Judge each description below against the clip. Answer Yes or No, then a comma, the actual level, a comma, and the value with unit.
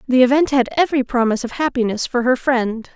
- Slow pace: No, fast, 205 wpm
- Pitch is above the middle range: Yes, very high, 250 Hz